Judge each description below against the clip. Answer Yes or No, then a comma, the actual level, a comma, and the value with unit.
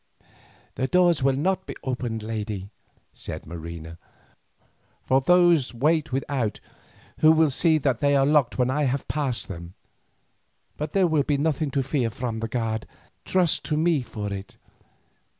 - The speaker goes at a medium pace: Yes, average, 155 wpm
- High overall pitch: No, low, 135 Hz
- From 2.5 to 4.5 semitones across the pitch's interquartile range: No, wide, 5.4 semitones